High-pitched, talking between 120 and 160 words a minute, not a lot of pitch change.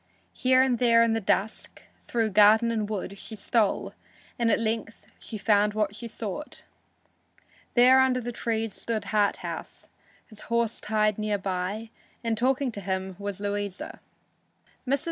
Yes: high, 220 Hz; average, 150 wpm; narrow, 2.3 semitones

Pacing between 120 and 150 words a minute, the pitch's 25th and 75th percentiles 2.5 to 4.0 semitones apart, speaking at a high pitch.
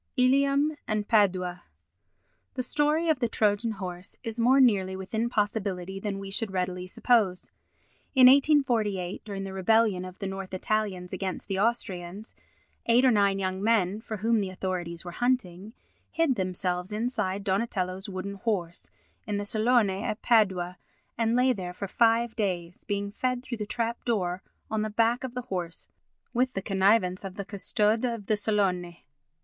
No: average, 165 wpm; average, 3.7 semitones; high, 205 Hz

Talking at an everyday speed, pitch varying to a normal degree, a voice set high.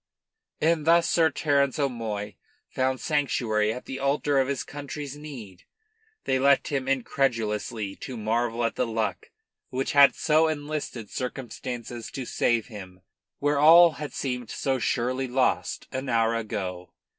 No: average, 145 wpm; average, 3.8 semitones; low, 130 Hz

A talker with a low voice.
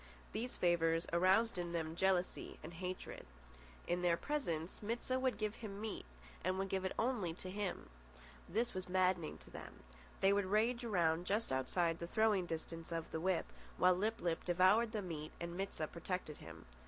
No: medium, 185 Hz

